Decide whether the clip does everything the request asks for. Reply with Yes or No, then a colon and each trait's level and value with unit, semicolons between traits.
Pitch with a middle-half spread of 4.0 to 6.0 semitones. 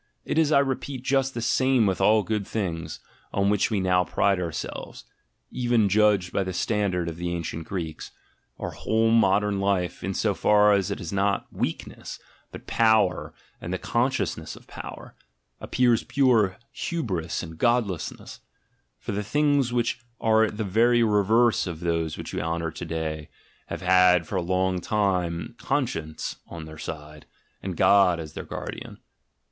Yes: average, 4.6 semitones